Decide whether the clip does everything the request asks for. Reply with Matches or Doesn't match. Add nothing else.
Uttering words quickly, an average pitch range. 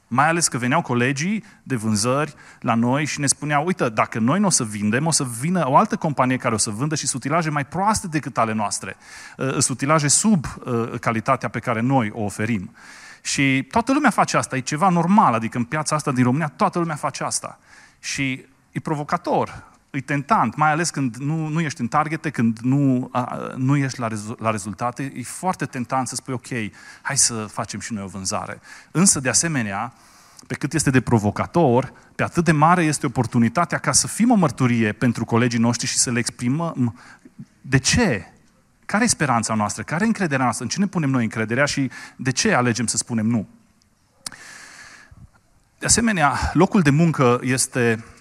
Matches